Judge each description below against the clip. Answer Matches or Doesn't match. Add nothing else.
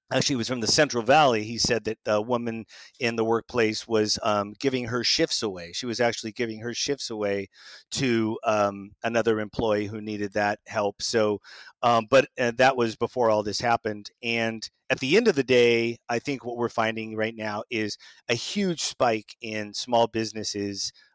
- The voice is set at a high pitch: Doesn't match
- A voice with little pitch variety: Matches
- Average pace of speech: Matches